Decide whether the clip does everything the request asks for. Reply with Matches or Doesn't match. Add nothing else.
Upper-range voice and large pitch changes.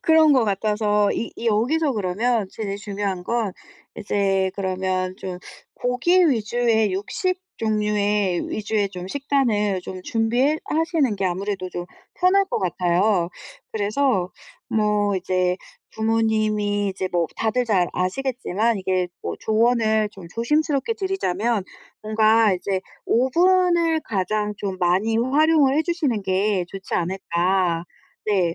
Doesn't match